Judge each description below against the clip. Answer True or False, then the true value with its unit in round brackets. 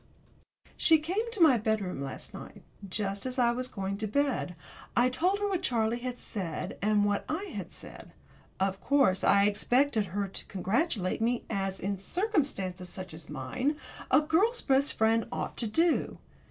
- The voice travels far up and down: True (6.7 semitones)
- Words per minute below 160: False (170 wpm)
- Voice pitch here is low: False (225 Hz)